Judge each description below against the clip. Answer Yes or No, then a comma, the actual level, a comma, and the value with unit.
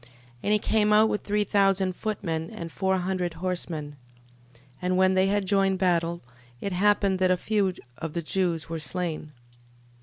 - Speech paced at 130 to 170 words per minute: No, average, 180 wpm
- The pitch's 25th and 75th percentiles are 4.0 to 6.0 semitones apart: No, average, 2.7 semitones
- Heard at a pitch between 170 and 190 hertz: Yes, medium, 185 Hz